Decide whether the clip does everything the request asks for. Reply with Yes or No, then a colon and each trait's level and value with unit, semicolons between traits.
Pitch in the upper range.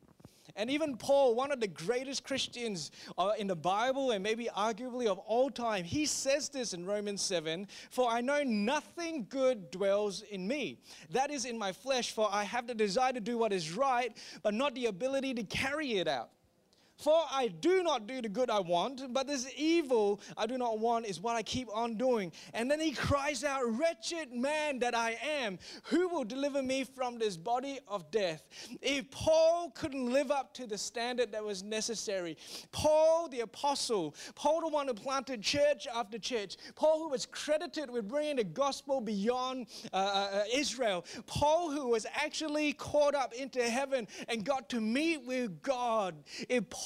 Yes: very high, 255 Hz